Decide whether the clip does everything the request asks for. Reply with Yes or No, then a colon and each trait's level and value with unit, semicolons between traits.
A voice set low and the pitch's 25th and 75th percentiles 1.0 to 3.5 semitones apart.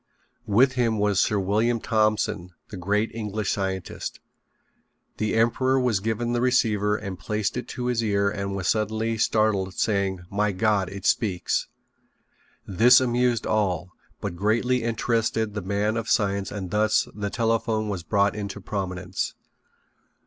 Yes: low, 105 Hz; narrow, 2.5 semitones